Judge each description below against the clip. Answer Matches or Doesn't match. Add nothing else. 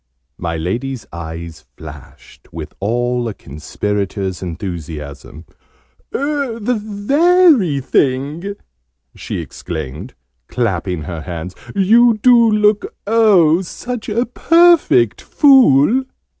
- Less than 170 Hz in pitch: Matches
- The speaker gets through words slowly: Matches